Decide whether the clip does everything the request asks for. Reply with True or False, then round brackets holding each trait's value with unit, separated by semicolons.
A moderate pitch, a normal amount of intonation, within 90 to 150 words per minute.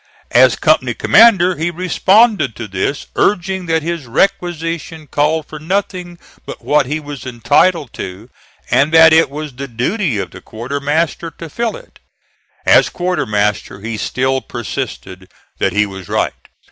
False (150 Hz; 6.1 semitones; 145 wpm)